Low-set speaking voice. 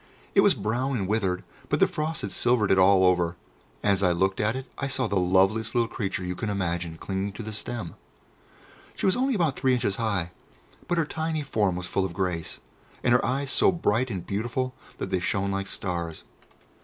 Yes: low, 100 Hz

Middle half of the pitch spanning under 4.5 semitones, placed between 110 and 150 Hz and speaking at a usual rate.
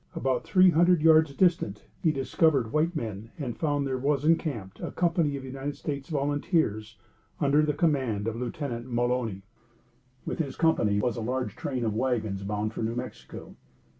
No: average, 5.1 semitones; low, 135 Hz; average, 165 wpm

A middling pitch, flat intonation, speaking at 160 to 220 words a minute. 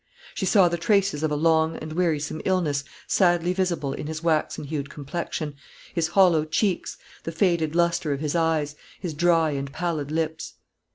Yes: medium, 160 Hz; narrow, 2.3 semitones; average, 170 wpm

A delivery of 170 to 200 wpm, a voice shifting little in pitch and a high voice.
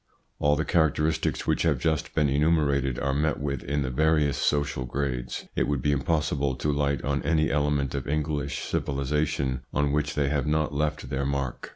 No: average, 190 wpm; narrow, 1.5 semitones; very low, 70 Hz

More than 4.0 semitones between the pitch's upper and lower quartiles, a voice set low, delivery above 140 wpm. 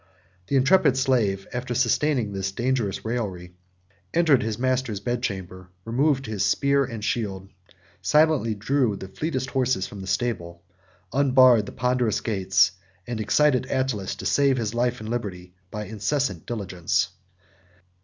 No: average, 4.9 semitones; low, 120 Hz; slow, 135 wpm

